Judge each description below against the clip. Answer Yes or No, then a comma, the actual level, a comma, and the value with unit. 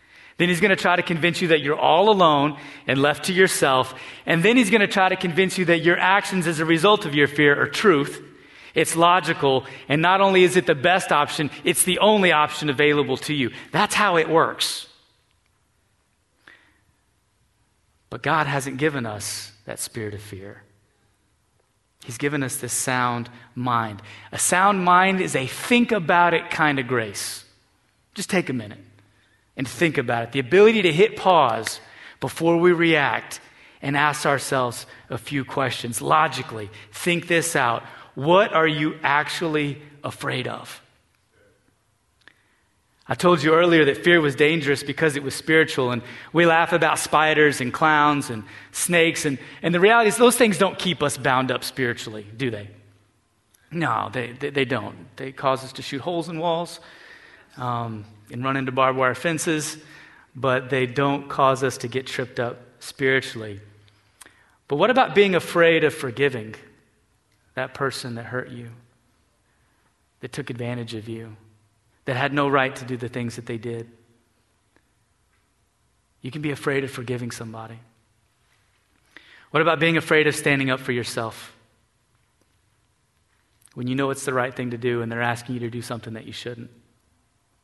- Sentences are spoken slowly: No, average, 165 wpm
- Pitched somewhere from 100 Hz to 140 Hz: Yes, low, 135 Hz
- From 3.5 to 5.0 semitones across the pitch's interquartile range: No, wide, 5.6 semitones